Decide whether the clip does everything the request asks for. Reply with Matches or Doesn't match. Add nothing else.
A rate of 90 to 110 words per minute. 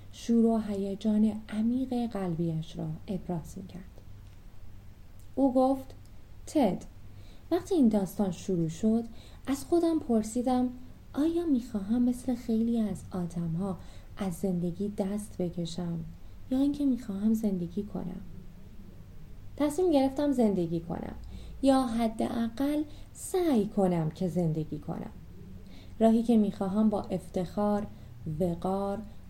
Matches